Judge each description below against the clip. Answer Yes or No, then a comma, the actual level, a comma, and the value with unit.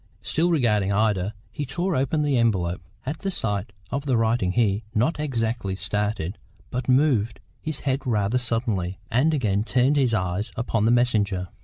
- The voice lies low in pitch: Yes, low, 115 Hz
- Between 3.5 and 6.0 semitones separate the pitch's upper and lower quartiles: Yes, average, 4.7 semitones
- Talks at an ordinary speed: Yes, average, 165 wpm